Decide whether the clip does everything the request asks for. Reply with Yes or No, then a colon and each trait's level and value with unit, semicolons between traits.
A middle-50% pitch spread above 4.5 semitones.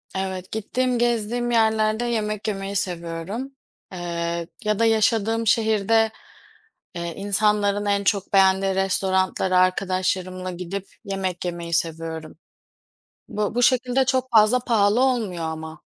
No: average, 3.4 semitones